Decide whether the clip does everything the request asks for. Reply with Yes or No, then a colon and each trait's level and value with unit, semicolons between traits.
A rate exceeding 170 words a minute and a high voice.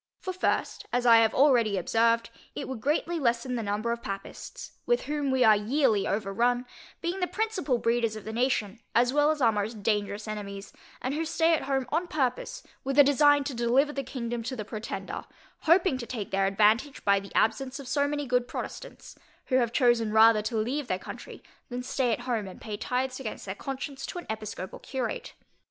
Yes: fast, 205 wpm; high, 245 Hz